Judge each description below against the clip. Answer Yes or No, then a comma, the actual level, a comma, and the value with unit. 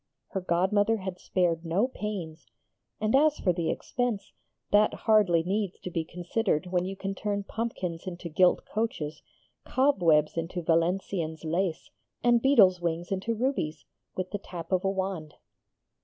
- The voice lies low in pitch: No, medium, 185 Hz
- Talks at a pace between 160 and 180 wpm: No, average, 150 wpm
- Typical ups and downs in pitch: Yes, average, 3.8 semitones